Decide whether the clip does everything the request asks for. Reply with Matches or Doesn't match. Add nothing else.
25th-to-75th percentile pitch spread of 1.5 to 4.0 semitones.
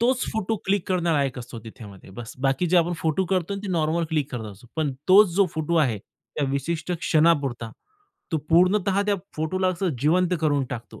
Doesn't match